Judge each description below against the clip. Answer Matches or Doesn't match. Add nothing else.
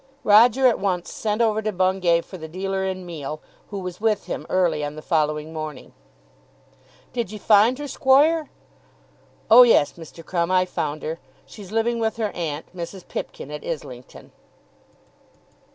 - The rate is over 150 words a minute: Matches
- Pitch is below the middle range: Doesn't match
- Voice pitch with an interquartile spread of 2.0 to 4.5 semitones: Doesn't match